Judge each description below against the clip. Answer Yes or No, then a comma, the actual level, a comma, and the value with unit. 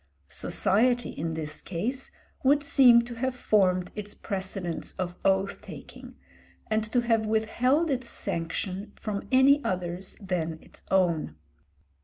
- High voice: Yes, high, 205 Hz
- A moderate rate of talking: No, slow, 130 wpm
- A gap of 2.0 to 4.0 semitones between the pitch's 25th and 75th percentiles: No, average, 5.1 semitones